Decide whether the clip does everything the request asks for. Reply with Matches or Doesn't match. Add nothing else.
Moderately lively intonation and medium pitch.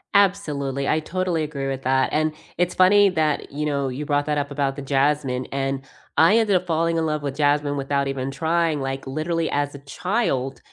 Matches